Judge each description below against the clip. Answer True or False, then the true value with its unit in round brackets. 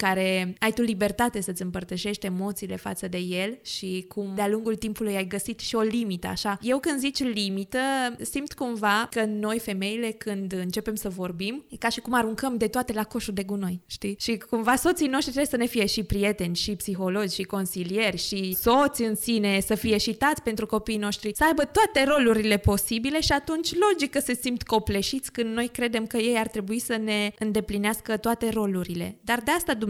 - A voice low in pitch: False (220 Hz)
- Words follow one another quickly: True (195 wpm)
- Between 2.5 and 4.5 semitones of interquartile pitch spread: True (3.1 semitones)